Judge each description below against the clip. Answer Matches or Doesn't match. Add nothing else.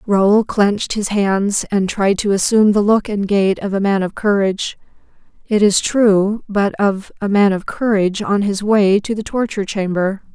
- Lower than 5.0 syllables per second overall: Matches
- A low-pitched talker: Doesn't match